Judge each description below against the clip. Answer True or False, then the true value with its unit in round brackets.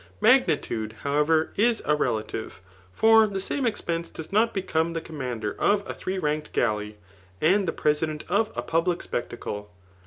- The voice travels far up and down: True (6.7 semitones)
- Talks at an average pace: True (160 wpm)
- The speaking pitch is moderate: True (160 Hz)